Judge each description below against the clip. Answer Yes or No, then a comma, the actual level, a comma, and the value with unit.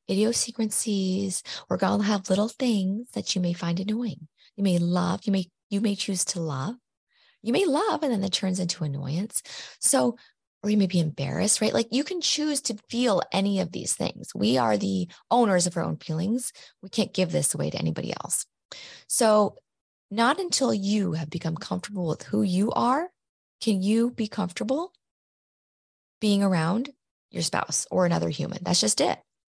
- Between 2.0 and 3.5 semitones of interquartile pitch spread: No, average, 4.0 semitones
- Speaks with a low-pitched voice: No, high, 200 Hz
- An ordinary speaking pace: Yes, average, 185 wpm